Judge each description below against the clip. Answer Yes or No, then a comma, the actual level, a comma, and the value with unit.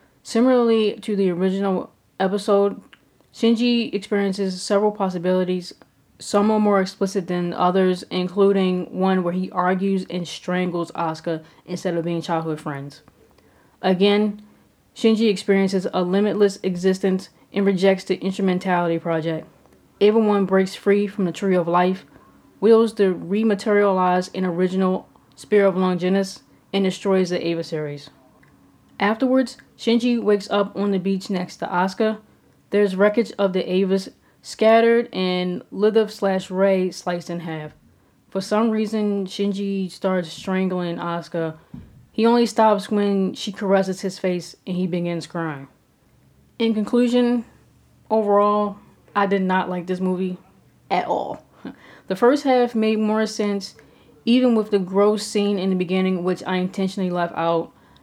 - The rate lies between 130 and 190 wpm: Yes, average, 140 wpm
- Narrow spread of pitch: Yes, narrow, 2.3 semitones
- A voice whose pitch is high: Yes, high, 195 Hz